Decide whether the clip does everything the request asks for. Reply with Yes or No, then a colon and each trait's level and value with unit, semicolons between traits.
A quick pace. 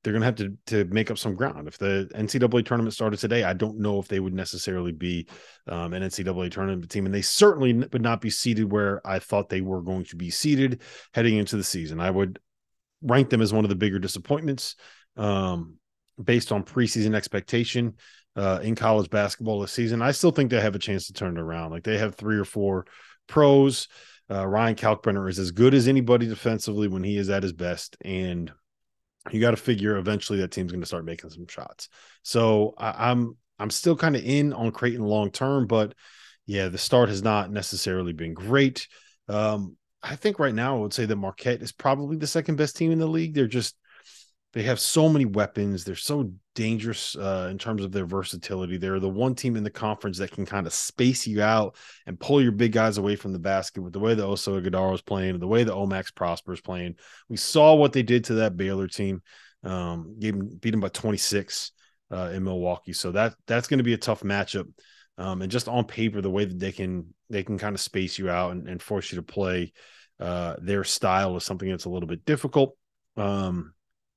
Yes: fast, 220 wpm